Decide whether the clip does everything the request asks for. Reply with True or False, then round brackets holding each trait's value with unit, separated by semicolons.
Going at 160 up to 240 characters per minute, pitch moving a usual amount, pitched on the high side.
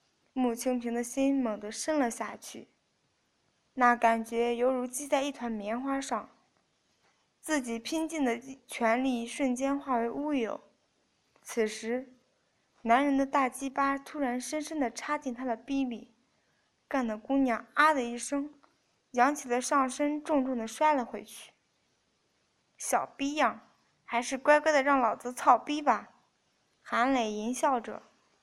True (200 characters per minute; 3.0 semitones; 255 Hz)